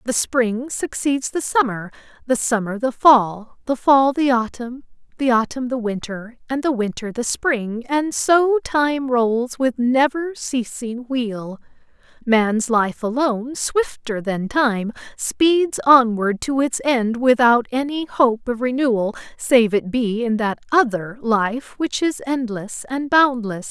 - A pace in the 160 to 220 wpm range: No, average, 145 wpm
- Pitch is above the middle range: Yes, high, 245 Hz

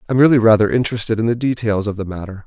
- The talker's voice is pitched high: No, low, 110 Hz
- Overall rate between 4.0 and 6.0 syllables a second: No, 7.9 syllables/s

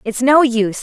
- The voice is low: No, high, 245 Hz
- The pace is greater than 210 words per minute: Yes, fast, 220 wpm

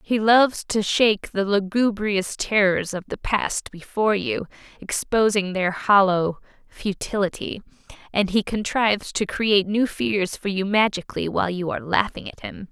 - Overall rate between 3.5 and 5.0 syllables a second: Yes, 4.7 syllables/s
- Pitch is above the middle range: Yes, high, 200 Hz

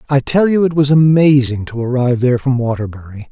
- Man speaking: Yes, male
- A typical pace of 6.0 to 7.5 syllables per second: Yes, 6.1 syllables/s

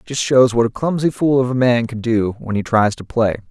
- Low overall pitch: Yes, low, 120 Hz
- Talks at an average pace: No, fast, 275 wpm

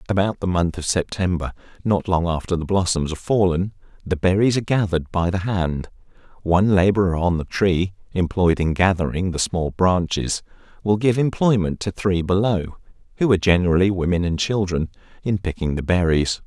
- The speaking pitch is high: No, very low, 90 Hz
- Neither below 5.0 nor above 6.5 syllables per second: No, 4.8 syllables/s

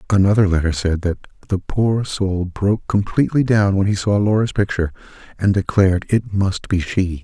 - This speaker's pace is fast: No, average, 175 wpm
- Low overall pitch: Yes, very low, 95 Hz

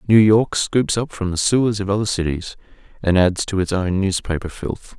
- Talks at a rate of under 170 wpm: No, fast, 205 wpm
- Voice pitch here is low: Yes, low, 100 Hz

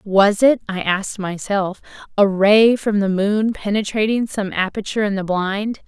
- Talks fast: No, average, 165 wpm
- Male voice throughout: No, female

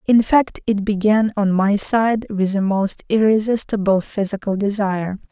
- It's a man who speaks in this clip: No, female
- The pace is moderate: Yes, average, 145 wpm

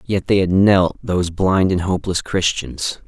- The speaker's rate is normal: Yes, average, 175 wpm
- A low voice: Yes, very low, 90 Hz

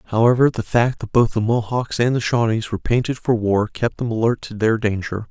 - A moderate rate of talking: No, fast, 225 wpm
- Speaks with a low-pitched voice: Yes, low, 115 Hz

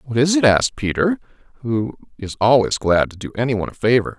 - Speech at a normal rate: No, fast, 215 wpm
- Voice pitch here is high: No, low, 120 Hz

